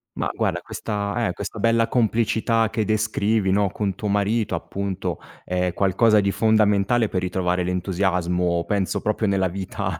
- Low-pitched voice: Yes, low, 100 Hz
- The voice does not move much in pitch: No, average, 3.0 semitones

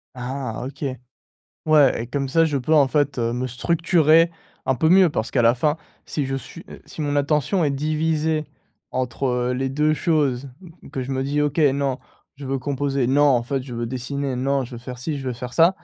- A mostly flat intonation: No, average, 3.0 semitones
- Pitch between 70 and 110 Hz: No, medium, 140 Hz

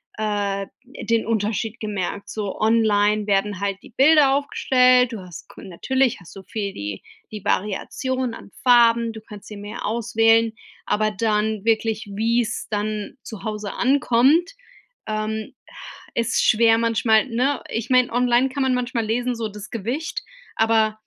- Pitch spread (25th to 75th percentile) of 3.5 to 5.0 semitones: No, narrow, 2.5 semitones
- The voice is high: Yes, high, 225 Hz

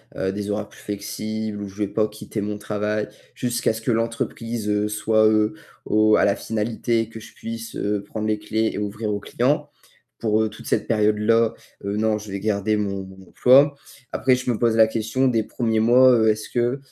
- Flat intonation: Yes, narrow, 1.5 semitones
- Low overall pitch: Yes, low, 110 Hz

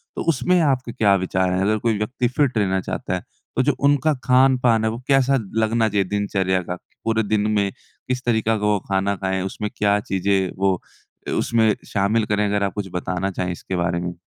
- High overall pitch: No, low, 105 Hz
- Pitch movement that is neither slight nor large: Yes, average, 3.5 semitones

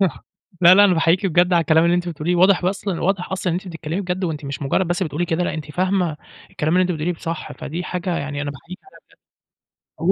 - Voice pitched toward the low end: No, medium, 175 Hz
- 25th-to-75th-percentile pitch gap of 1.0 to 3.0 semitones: Yes, narrow, 2.4 semitones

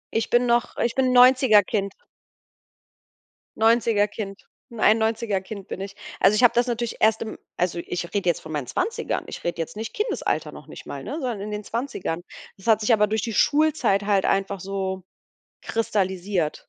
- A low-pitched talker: No, high, 210 Hz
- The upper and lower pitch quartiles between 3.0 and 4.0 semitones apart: Yes, average, 3.3 semitones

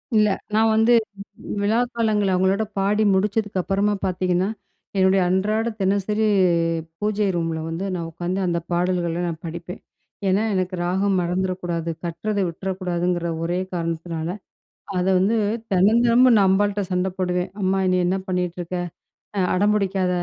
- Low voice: No, medium, 185 Hz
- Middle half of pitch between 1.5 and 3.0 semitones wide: Yes, narrow, 2.5 semitones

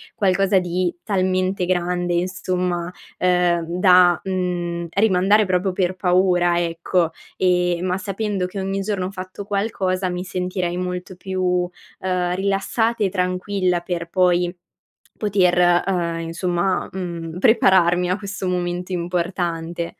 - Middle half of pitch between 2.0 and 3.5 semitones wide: No, narrow, 1.3 semitones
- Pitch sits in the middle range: Yes, medium, 180 Hz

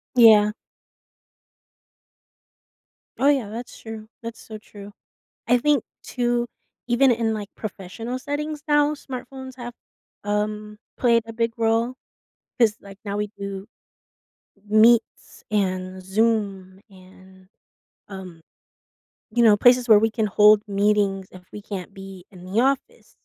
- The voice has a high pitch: Yes, high, 215 Hz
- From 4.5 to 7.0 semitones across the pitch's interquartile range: No, average, 3.3 semitones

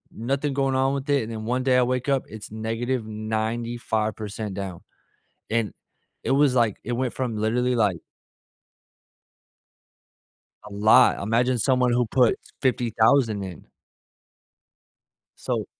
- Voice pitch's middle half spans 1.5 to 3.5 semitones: Yes, average, 2.8 semitones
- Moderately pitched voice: No, low, 120 Hz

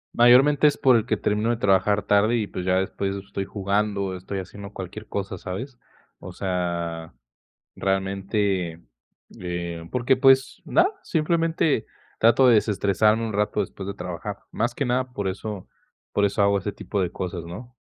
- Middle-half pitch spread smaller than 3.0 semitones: No, average, 3.9 semitones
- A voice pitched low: Yes, low, 100 Hz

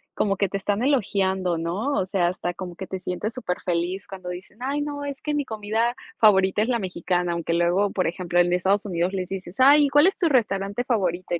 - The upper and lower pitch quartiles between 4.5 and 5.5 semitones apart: Yes, average, 4.8 semitones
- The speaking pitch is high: Yes, high, 195 Hz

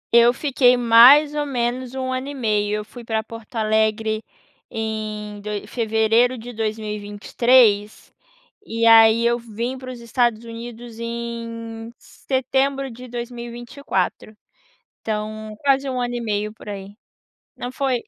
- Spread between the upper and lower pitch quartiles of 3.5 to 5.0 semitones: No, narrow, 2.4 semitones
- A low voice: No, high, 230 Hz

